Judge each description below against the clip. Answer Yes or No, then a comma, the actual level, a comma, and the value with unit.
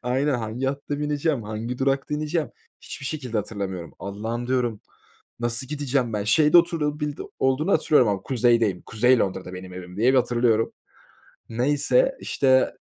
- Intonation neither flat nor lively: Yes, average, 4.7 semitones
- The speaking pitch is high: No, low, 125 Hz